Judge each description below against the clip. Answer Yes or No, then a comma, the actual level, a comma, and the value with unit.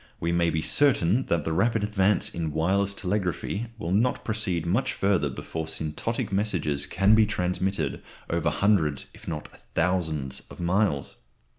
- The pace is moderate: Yes, average, 150 wpm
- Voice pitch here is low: Yes, very low, 90 Hz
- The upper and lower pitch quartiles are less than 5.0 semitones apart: Yes, average, 4.3 semitones